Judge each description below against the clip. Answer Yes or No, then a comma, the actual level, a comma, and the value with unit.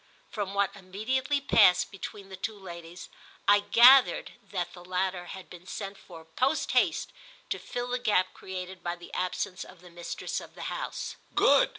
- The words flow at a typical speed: Yes, average, 175 wpm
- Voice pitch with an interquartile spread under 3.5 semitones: Yes, average, 2.7 semitones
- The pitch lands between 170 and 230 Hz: Yes, high, 190 Hz